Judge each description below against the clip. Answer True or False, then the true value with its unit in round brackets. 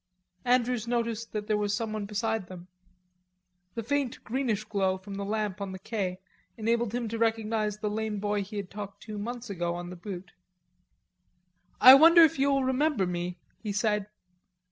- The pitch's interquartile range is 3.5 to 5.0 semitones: False (2.7 semitones)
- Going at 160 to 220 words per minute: True (170 wpm)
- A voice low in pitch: False (215 Hz)